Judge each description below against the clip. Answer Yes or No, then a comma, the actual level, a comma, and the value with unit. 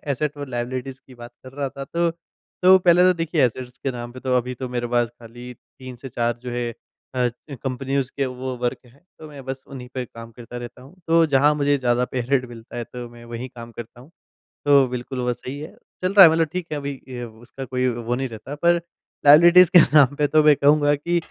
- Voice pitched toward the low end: Yes, low, 130 Hz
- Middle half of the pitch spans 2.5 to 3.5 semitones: Yes, average, 3.0 semitones